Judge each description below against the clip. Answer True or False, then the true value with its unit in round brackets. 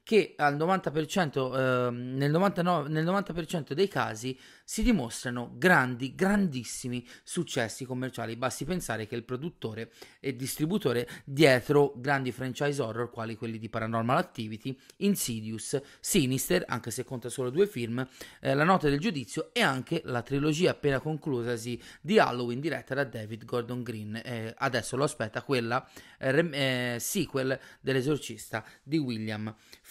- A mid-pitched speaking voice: False (130 Hz)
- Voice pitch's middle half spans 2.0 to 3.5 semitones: False (4.3 semitones)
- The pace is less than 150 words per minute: True (135 wpm)